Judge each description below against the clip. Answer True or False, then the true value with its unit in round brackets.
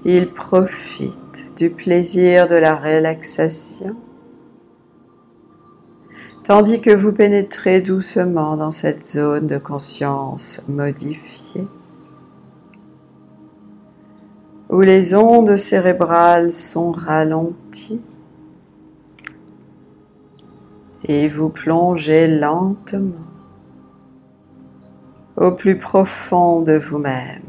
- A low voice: False (165 Hz)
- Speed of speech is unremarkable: False (70 wpm)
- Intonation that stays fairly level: False (4.6 semitones)